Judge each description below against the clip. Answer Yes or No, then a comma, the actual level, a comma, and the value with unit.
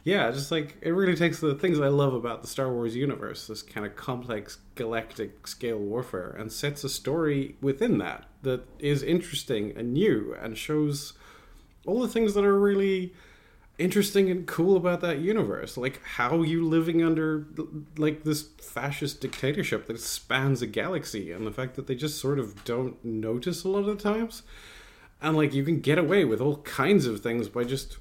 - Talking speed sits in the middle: Yes, average, 190 wpm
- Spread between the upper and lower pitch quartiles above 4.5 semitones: Yes, wide, 5.5 semitones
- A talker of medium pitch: Yes, medium, 145 Hz